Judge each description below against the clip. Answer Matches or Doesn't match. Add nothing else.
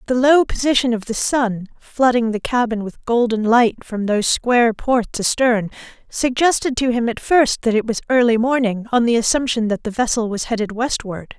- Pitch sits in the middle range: Doesn't match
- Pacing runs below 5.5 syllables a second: Matches